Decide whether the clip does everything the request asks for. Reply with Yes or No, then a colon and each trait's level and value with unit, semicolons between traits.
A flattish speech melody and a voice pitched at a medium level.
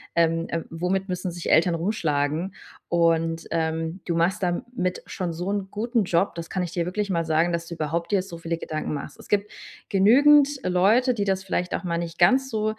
No: average, 3.0 semitones; medium, 175 Hz